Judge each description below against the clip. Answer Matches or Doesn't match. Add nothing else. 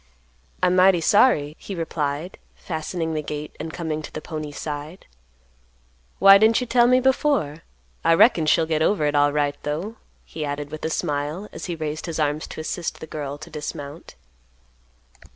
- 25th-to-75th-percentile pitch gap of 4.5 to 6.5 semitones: Doesn't match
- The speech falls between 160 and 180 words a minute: Matches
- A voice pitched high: Doesn't match